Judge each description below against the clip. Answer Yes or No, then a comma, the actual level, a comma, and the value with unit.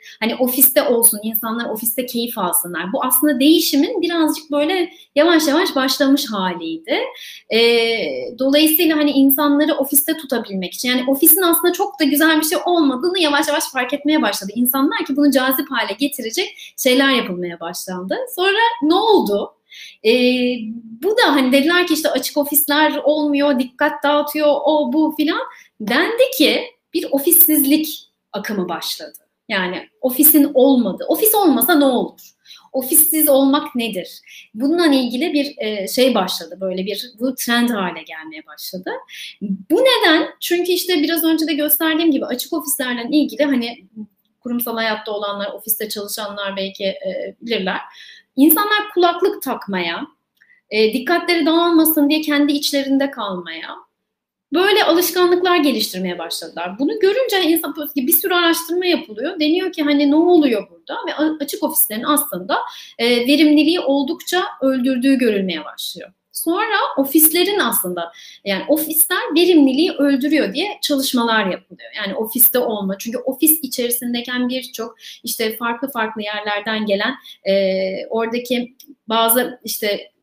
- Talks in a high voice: Yes, very high, 280 Hz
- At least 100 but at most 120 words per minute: No, average, 130 wpm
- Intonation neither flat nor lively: No, wide, 5.8 semitones